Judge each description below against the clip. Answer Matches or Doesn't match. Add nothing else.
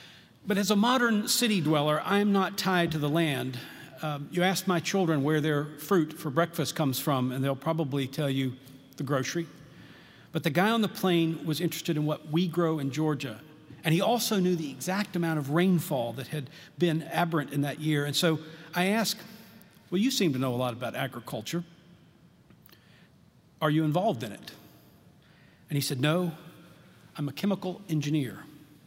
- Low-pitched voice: Doesn't match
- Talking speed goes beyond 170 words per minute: Matches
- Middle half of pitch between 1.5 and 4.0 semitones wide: Matches